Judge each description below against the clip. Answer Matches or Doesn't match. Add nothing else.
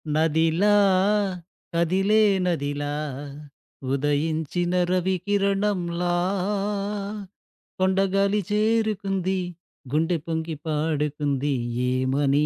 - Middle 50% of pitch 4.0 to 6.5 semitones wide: Matches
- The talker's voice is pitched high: Doesn't match